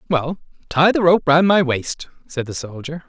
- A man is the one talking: Yes, male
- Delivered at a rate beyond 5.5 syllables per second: No, 4.7 syllables/s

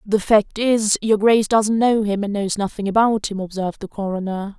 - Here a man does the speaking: No, female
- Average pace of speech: No, fast, 210 wpm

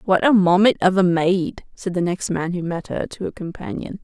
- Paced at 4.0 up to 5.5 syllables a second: Yes, 5.0 syllables/s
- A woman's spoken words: Yes, female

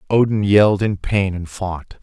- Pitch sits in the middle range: No, low, 100 Hz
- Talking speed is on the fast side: No, average, 175 wpm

